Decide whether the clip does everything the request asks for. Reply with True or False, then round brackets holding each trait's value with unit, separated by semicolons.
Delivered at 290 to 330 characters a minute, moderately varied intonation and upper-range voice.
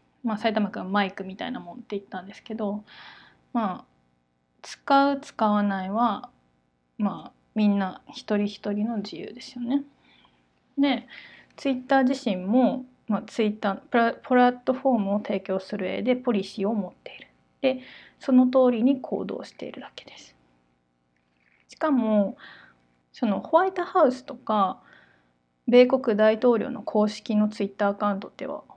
True (300 characters per minute; 4.6 semitones; 215 Hz)